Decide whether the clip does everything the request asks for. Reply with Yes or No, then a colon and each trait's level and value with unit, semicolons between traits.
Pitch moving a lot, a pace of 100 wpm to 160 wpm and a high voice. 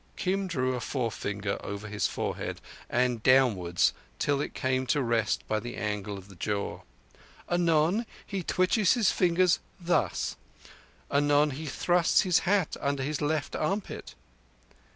No: wide, 7.7 semitones; average, 140 wpm; medium, 140 Hz